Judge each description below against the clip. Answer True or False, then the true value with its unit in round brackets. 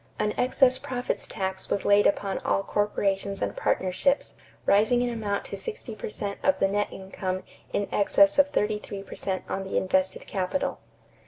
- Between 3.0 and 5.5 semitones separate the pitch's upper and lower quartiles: False (2.6 semitones)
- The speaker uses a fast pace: False (175 wpm)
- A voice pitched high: True (200 Hz)